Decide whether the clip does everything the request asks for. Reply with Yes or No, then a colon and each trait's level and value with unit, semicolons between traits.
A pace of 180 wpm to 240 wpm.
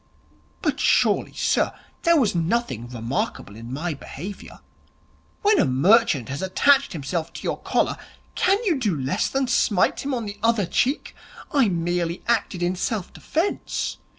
No: average, 150 wpm